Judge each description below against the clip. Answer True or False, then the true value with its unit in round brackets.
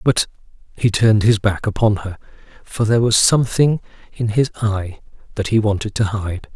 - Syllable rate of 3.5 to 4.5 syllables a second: False (5.3 syllables/s)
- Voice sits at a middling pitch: False (110 Hz)